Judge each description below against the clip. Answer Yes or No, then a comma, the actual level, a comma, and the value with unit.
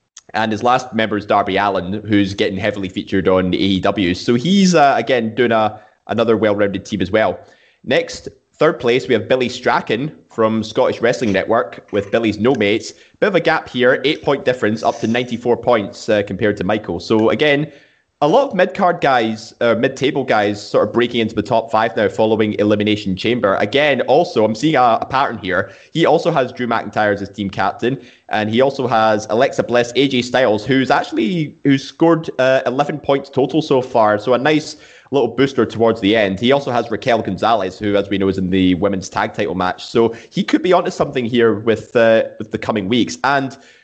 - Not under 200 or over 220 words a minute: Yes, fast, 205 wpm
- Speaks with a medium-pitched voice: No, low, 115 Hz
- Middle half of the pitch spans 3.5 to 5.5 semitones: Yes, average, 4.1 semitones